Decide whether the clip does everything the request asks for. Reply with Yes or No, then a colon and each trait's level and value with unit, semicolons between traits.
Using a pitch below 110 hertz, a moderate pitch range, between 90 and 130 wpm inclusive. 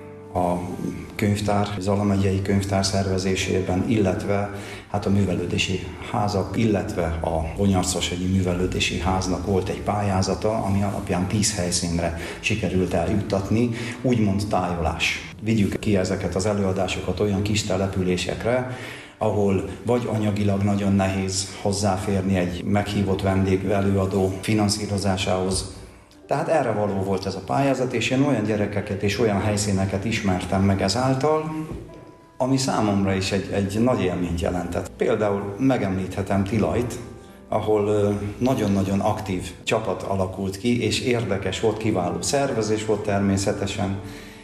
No: low, 100 Hz; narrow, 2.1 semitones; average, 115 wpm